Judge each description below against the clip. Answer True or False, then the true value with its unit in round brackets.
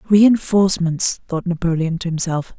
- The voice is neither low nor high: True (180 Hz)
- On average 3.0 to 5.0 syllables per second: True (4.8 syllables/s)